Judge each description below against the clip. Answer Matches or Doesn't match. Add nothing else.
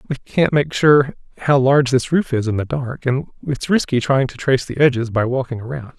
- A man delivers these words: Matches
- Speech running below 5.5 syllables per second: Doesn't match